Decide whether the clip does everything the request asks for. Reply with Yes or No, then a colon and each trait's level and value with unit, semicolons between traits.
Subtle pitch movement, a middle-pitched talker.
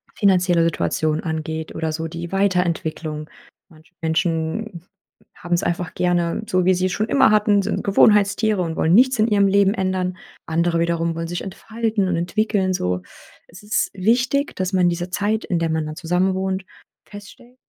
No: average, 3.3 semitones; medium, 180 Hz